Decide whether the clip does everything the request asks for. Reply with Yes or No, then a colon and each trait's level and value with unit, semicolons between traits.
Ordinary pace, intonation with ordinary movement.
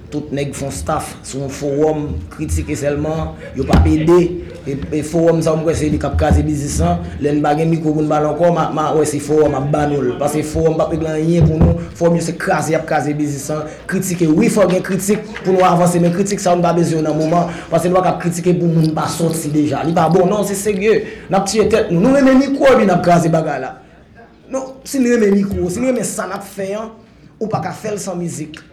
No: slow, 105 wpm; average, 4.0 semitones